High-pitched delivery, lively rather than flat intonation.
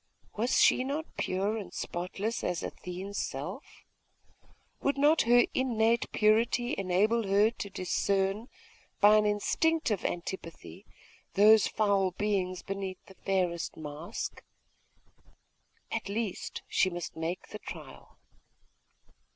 No: high, 200 Hz; average, 3.4 semitones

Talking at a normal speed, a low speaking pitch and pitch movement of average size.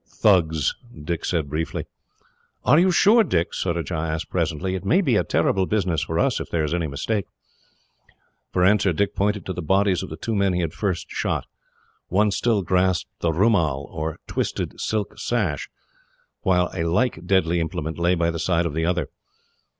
Yes: average, 180 wpm; very low, 90 Hz; average, 3.4 semitones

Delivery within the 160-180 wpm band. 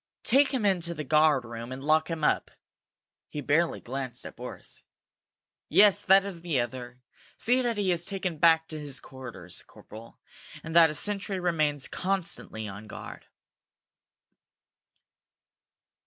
No: average, 140 wpm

